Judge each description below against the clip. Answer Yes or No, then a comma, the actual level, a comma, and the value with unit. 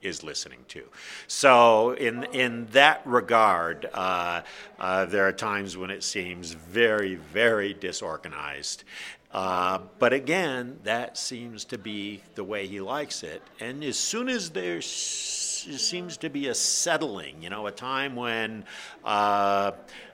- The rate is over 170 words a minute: No, average, 145 wpm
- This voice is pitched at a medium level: No, low, 110 Hz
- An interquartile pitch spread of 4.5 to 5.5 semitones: Yes, average, 5.2 semitones